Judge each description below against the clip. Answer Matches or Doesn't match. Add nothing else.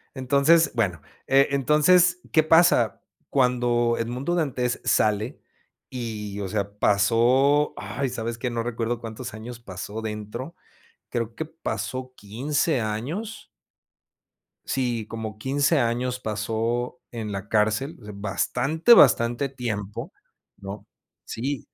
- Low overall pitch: Matches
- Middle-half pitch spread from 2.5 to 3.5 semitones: Doesn't match